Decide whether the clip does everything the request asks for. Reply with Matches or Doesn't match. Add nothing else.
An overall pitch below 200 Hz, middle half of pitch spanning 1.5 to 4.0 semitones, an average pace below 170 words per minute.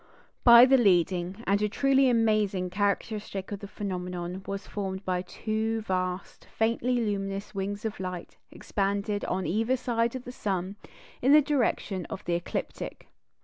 Doesn't match